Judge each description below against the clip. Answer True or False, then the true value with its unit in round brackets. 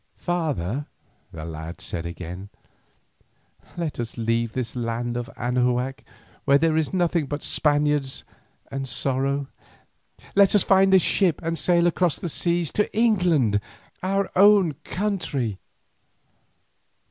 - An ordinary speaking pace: False (125 wpm)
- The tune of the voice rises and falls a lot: True (6.5 semitones)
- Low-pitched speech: False (145 Hz)